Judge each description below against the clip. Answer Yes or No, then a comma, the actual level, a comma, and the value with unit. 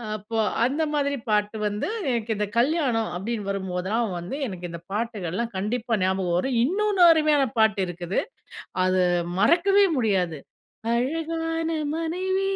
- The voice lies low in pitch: No, high, 230 Hz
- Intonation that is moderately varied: No, wide, 8.1 semitones